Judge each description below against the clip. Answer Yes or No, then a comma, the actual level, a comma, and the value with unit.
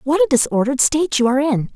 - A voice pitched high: Yes, very high, 270 Hz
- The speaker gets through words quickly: Yes, fast, 240 wpm